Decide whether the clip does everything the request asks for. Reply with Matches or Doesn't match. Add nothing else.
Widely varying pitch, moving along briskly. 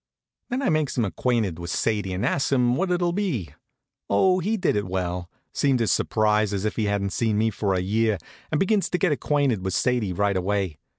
Matches